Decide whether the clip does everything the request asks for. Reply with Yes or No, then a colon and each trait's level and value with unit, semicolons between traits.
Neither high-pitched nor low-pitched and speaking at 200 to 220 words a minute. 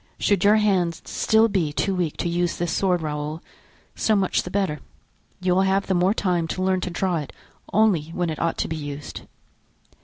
Yes: medium, 180 Hz; fast, 205 wpm